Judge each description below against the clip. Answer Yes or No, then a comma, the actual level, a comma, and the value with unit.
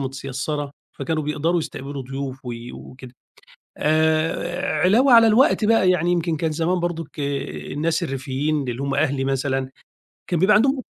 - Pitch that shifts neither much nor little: Yes, average, 4.2 semitones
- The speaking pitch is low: No, medium, 155 Hz